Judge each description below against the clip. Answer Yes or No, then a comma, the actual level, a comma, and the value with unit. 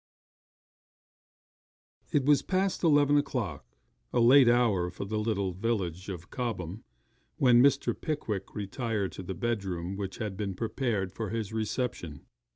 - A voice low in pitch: Yes, low, 110 Hz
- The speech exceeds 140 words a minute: No, slow, 135 wpm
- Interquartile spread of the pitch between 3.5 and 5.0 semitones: Yes, average, 4.6 semitones